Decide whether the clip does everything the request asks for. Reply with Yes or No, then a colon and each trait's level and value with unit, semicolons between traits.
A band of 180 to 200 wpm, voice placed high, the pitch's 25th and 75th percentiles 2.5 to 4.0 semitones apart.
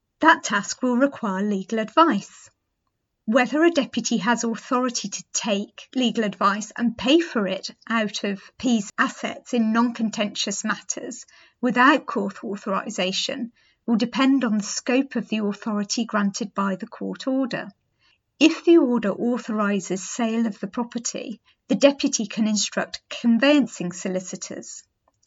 No: slow, 135 wpm; high, 230 Hz; average, 3.7 semitones